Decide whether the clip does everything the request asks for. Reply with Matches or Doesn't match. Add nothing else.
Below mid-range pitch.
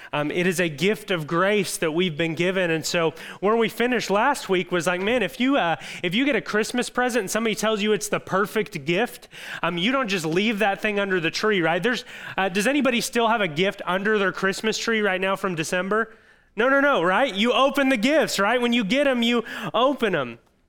Doesn't match